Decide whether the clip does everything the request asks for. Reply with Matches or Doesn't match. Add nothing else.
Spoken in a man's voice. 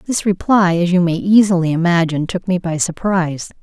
Doesn't match